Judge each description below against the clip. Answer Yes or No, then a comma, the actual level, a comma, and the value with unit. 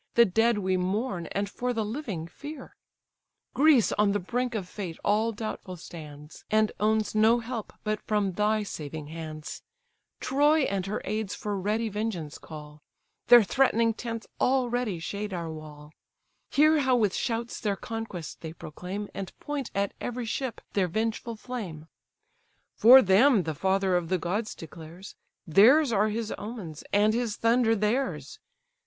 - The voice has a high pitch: Yes, high, 210 Hz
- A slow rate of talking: No, average, 155 wpm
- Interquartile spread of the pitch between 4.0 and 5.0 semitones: Yes, average, 4.4 semitones